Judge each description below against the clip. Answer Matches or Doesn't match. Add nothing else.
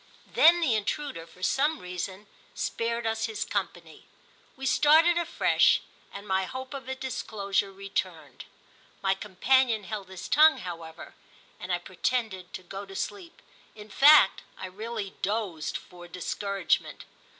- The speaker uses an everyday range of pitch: Doesn't match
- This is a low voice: Doesn't match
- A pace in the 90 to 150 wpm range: Matches